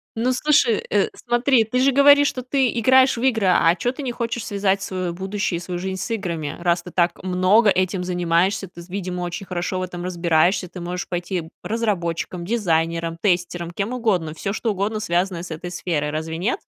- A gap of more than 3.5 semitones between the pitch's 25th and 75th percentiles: Yes, average, 4.3 semitones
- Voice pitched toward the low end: No, medium, 185 Hz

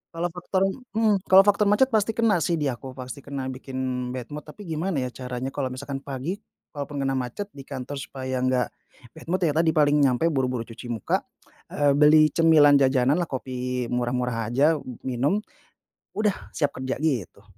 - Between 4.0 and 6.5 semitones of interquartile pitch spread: Yes, average, 4.5 semitones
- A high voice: No, medium, 140 Hz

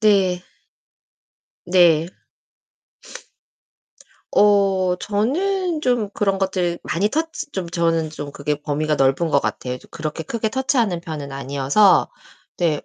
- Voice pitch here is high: No, medium, 180 Hz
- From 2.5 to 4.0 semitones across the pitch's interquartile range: No, average, 5.3 semitones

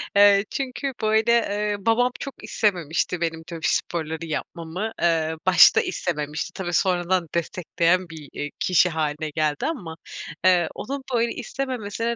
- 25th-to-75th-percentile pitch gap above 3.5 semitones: Yes, average, 5.0 semitones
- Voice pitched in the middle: Yes, medium, 180 Hz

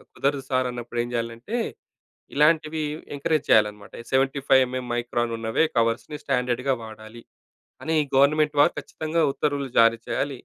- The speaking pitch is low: Yes, low, 130 Hz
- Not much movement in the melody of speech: No, average, 3.7 semitones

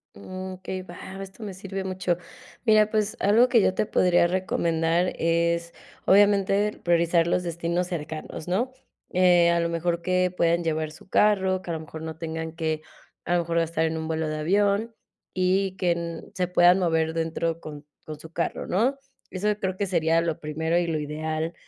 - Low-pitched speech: No, medium, 170 Hz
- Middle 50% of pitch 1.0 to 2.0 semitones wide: No, narrow, 2.6 semitones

